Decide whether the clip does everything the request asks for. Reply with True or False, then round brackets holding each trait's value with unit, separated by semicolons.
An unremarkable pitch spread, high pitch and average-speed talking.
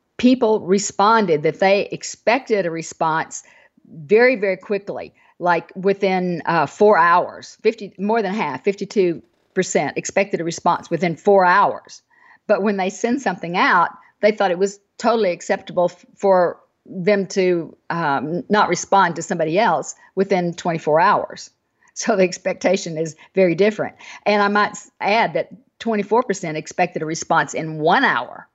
True (3.0 semitones; 195 Hz; 145 wpm)